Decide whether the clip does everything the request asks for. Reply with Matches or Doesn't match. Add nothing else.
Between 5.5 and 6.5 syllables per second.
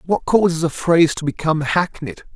Matches